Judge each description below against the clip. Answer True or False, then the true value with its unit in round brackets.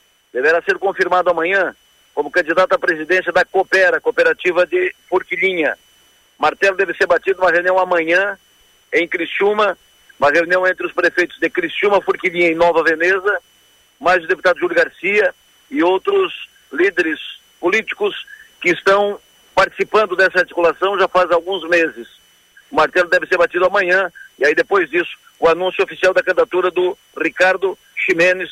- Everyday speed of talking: True (145 wpm)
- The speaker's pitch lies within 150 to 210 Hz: True (185 Hz)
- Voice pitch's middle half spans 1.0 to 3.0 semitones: True (2.6 semitones)